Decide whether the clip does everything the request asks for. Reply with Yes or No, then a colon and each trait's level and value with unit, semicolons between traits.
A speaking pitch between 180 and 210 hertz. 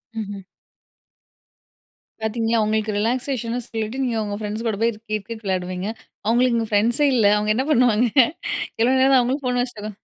No: high, 225 Hz